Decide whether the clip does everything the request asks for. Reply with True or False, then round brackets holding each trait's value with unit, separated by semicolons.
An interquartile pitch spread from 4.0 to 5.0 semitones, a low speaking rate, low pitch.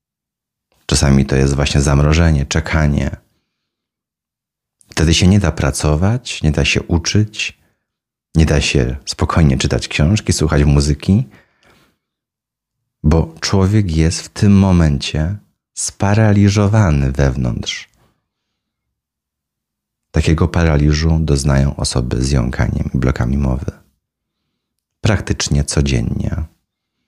True (4.6 semitones; 95 wpm; 75 Hz)